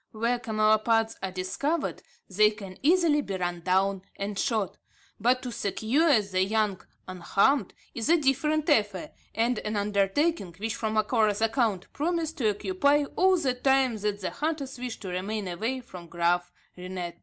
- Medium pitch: No, high, 220 Hz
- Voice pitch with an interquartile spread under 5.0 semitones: No, wide, 5.6 semitones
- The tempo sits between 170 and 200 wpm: No, average, 155 wpm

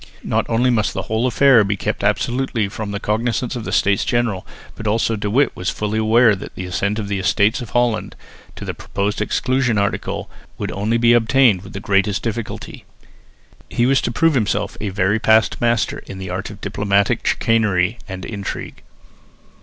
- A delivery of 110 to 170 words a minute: No, average, 185 wpm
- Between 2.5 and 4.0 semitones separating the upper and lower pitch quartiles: Yes, average, 2.9 semitones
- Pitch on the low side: Yes, low, 110 Hz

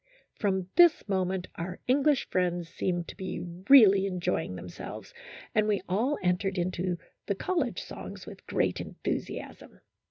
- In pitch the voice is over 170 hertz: Yes, high, 190 Hz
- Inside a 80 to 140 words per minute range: Yes, slow, 135 wpm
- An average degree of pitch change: Yes, average, 3.1 semitones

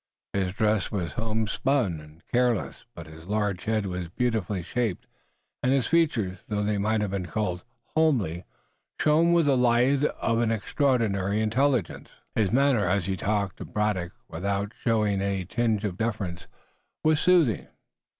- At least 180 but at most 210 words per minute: No, average, 150 wpm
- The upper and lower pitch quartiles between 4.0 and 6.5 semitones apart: Yes, average, 4.3 semitones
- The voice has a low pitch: Yes, low, 105 Hz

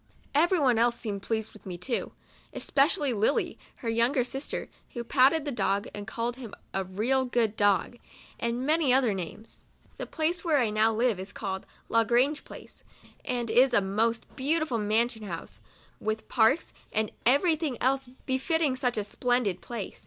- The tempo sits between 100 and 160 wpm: No, average, 175 wpm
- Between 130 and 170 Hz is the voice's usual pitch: No, high, 240 Hz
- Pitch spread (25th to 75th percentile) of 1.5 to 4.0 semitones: Yes, average, 3.7 semitones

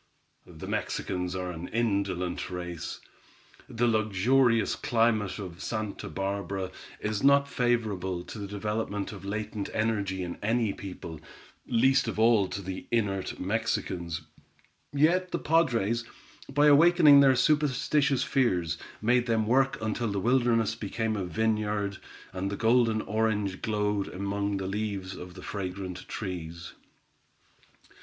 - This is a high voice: No, low, 105 Hz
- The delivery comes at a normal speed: No, slow, 130 wpm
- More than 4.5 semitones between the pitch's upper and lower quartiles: No, average, 3.7 semitones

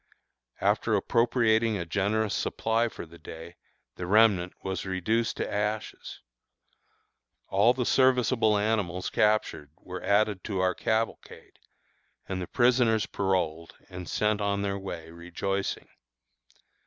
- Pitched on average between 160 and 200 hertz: No, low, 100 Hz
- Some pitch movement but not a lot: Yes, average, 3.3 semitones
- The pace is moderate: No, slow, 120 wpm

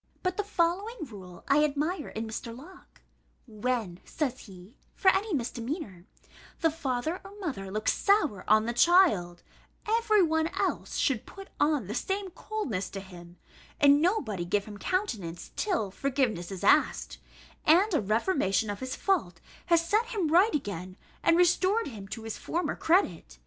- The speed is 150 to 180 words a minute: Yes, average, 160 wpm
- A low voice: No, very high, 275 Hz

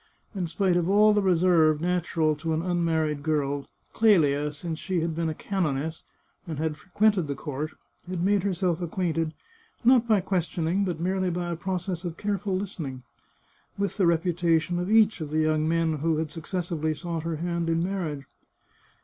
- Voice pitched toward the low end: No, medium, 170 Hz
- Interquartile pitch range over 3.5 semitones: No, average, 2.9 semitones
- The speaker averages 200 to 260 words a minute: No, average, 185 wpm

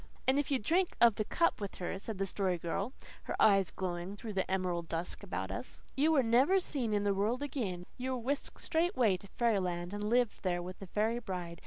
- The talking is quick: Yes, fast, 220 wpm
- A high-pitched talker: Yes, high, 205 Hz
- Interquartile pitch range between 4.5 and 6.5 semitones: Yes, average, 5.2 semitones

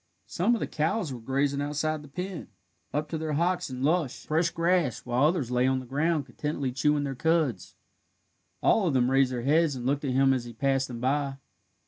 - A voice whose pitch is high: No, medium, 140 Hz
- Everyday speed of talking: No, fast, 210 wpm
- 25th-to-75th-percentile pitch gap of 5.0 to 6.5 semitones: No, average, 3.5 semitones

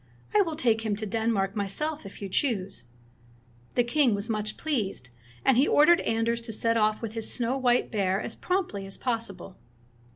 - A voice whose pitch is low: No, high, 225 Hz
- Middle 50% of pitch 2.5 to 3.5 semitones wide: No, average, 3.9 semitones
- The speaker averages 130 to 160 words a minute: No, average, 185 wpm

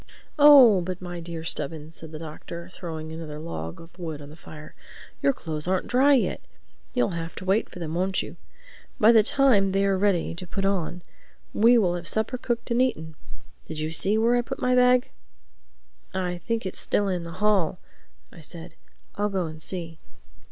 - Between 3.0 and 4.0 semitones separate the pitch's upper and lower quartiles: No, average, 4.5 semitones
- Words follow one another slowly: No, average, 195 wpm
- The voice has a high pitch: No, medium, 180 Hz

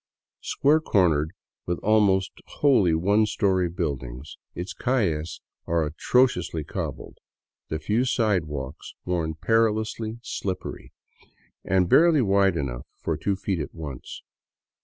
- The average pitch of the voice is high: No, very low, 95 Hz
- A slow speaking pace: Yes, slow, 115 wpm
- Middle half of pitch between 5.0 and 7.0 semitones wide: Yes, wide, 5.5 semitones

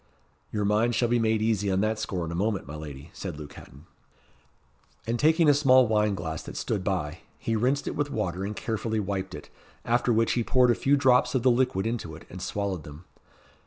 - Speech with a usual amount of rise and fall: Yes, average, 4.6 semitones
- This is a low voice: Yes, low, 105 Hz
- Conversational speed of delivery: No, fast, 220 wpm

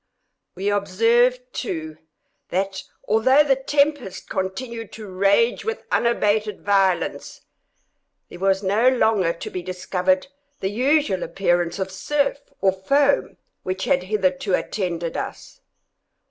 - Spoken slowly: Yes, slow, 120 wpm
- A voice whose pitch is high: Yes, high, 200 Hz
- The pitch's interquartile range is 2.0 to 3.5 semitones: No, average, 4.3 semitones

